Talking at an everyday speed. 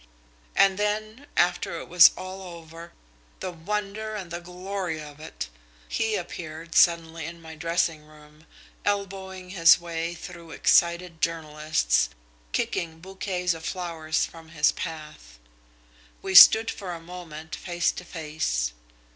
No: slow, 130 wpm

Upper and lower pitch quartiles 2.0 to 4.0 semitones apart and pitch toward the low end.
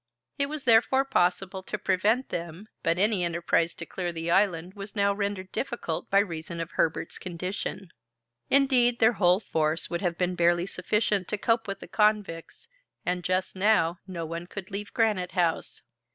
No: average, 3.6 semitones; medium, 185 Hz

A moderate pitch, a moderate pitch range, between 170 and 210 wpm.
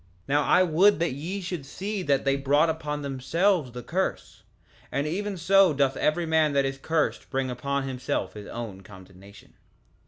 Yes: medium, 145 Hz; average, 4.3 semitones; average, 180 wpm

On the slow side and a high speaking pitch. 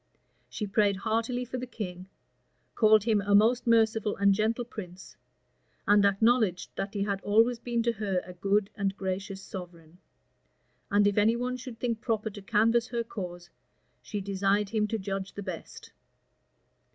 No: average, 165 wpm; high, 210 Hz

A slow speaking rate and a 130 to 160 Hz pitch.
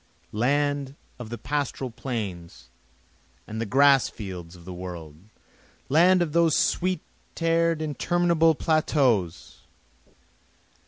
Yes: slow, 100 wpm; medium, 140 Hz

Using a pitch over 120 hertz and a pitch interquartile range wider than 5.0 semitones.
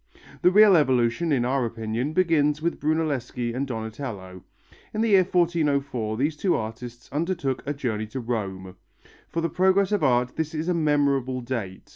Yes: medium, 140 Hz; wide, 5.6 semitones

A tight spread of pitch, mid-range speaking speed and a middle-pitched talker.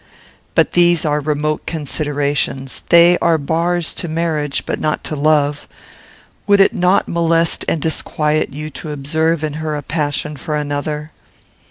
Yes: narrow, 2.1 semitones; average, 150 wpm; medium, 155 Hz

